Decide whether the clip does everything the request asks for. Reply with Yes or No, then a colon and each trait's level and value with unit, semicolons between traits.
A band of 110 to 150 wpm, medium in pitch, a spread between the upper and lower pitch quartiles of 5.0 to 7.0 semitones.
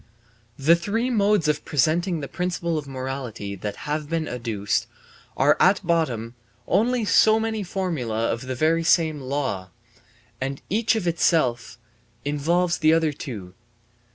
Yes: average, 140 wpm; medium, 155 Hz; wide, 5.6 semitones